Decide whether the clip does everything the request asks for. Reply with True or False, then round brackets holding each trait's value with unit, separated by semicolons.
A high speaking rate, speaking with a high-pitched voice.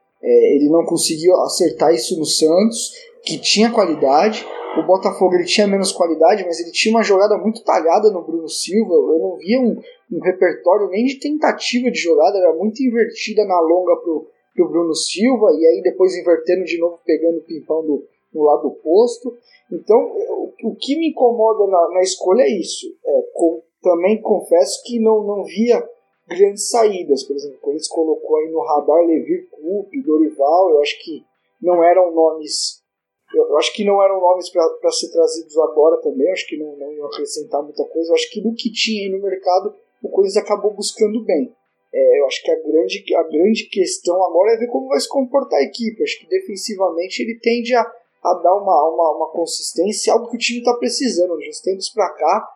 True (195 wpm; 210 Hz)